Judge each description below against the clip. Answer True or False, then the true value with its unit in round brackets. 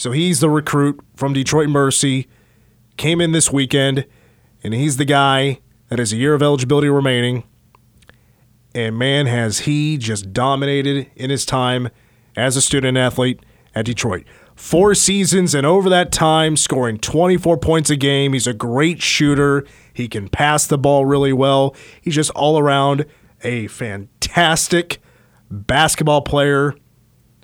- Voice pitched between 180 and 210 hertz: False (140 Hz)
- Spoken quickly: False (145 wpm)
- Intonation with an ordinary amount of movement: True (3.5 semitones)